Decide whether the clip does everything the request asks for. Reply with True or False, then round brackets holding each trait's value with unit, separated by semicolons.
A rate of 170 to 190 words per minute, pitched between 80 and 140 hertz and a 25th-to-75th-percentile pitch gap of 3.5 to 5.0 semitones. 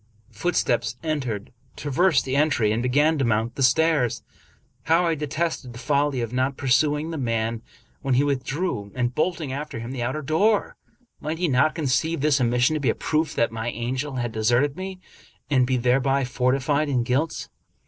True (185 wpm; 135 Hz; 4.0 semitones)